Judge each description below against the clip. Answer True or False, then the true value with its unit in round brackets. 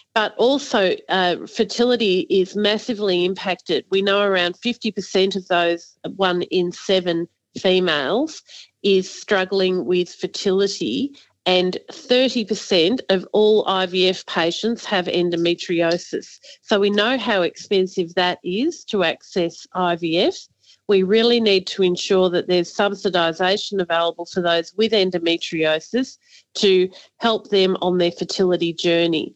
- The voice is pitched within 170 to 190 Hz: True (185 Hz)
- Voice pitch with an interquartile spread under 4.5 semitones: True (2.9 semitones)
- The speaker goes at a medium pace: False (120 wpm)